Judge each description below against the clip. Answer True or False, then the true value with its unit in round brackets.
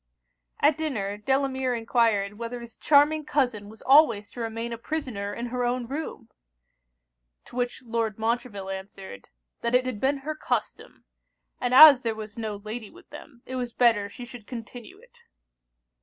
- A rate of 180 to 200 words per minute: False (165 wpm)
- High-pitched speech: True (240 Hz)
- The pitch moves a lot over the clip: False (3.4 semitones)